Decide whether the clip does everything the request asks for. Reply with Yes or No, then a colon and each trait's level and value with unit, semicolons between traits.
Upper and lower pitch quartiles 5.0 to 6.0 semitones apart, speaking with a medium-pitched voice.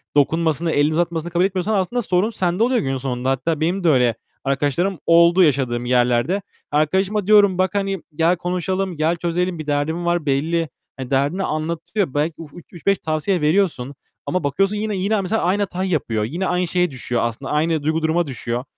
No: average, 4.4 semitones; medium, 170 Hz